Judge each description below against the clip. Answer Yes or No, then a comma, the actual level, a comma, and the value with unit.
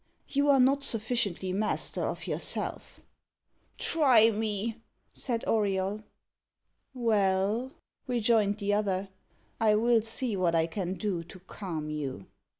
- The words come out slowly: Yes, slow, 120 wpm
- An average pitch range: Yes, average, 3.5 semitones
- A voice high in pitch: Yes, high, 210 Hz